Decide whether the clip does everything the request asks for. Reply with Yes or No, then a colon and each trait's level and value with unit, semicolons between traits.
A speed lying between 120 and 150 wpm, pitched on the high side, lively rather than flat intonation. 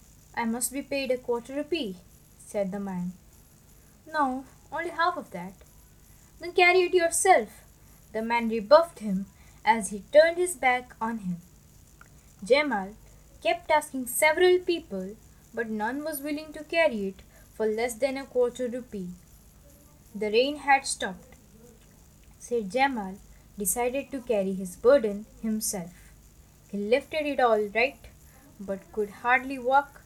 Yes: average, 140 wpm; high, 245 Hz; wide, 6.3 semitones